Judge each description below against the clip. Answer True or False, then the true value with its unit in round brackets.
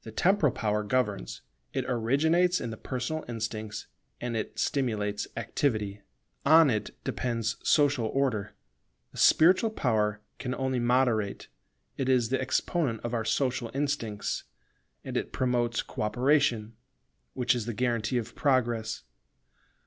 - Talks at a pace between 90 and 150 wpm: True (135 wpm)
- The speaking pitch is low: True (120 Hz)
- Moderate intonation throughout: True (3.5 semitones)